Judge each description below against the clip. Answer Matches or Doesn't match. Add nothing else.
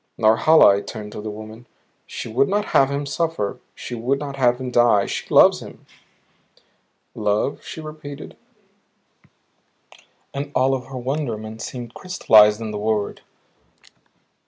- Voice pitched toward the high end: Doesn't match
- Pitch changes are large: Doesn't match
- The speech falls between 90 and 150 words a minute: Matches